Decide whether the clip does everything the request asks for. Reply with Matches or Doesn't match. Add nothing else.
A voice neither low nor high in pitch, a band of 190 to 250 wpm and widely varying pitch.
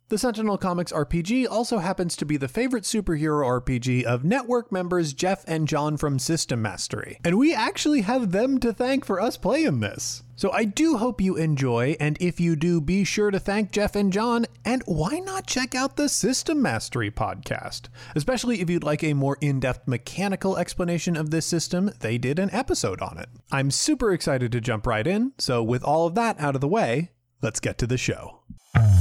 Matches